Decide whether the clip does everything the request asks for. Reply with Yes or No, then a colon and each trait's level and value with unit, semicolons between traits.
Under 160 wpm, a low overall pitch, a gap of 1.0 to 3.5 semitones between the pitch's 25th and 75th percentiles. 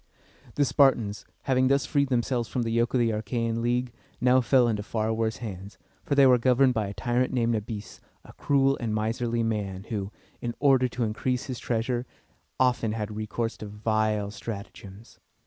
No: average, 180 wpm; low, 115 Hz; average, 2.8 semitones